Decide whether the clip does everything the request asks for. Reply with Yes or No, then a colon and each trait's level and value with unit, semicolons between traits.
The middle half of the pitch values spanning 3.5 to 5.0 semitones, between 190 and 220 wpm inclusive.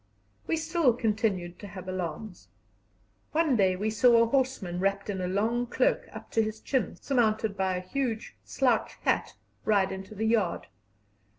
No: average, 4.0 semitones; average, 165 wpm